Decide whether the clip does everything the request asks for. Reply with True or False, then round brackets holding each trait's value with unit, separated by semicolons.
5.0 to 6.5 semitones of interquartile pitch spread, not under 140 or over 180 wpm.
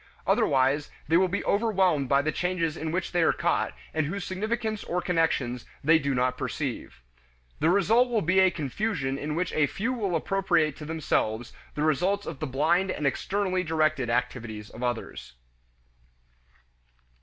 True (5.3 semitones; 165 wpm)